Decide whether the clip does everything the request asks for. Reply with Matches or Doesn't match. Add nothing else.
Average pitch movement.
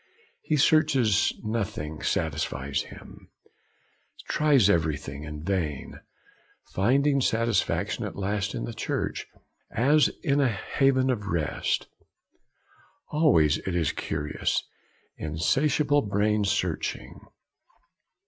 Doesn't match